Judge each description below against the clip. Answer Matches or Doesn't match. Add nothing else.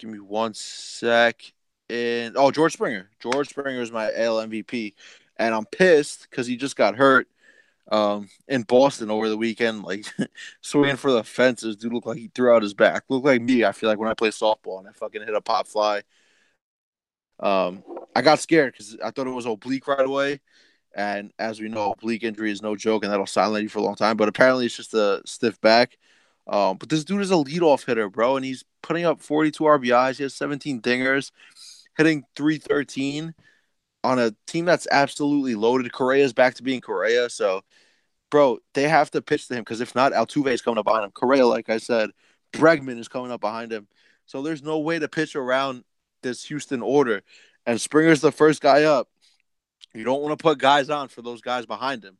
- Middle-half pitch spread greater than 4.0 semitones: Matches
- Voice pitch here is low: Matches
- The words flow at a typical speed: Doesn't match